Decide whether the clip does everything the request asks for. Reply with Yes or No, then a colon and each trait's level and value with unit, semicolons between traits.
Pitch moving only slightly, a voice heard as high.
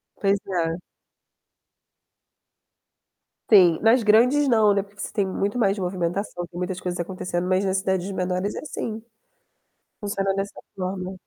Yes: narrow, 2.0 semitones; high, 195 Hz